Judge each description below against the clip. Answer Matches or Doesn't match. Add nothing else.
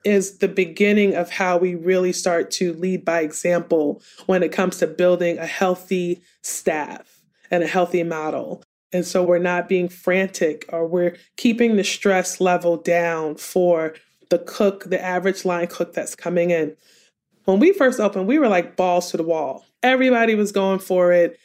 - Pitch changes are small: Matches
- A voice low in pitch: Doesn't match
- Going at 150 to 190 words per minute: Matches